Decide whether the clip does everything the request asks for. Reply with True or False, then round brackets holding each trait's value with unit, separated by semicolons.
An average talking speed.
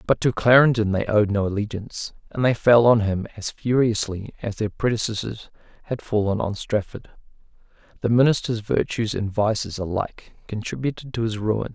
True (160 wpm)